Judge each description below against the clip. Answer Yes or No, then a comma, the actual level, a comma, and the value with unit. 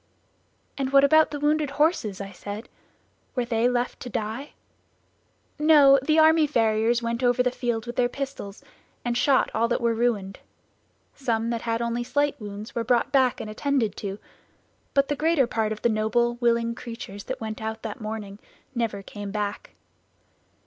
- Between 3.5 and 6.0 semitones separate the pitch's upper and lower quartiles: Yes, average, 3.8 semitones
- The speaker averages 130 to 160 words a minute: No, average, 170 wpm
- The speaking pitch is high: Yes, high, 235 Hz